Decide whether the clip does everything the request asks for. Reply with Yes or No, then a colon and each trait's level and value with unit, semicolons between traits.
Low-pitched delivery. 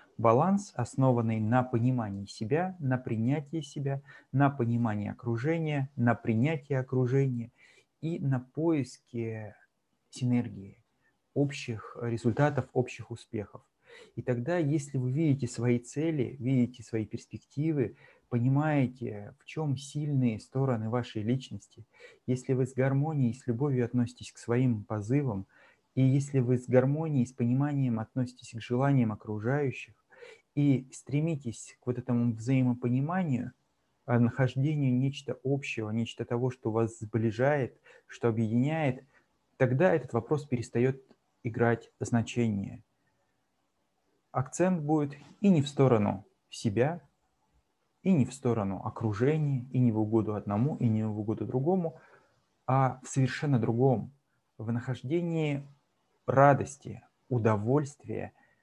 Yes: low, 125 Hz